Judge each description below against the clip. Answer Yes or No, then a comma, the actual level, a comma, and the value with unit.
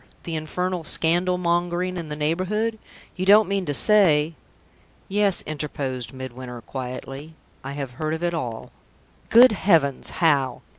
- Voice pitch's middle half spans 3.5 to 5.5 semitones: Yes, average, 4.7 semitones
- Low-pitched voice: No, medium, 160 Hz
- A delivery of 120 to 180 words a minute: Yes, average, 145 wpm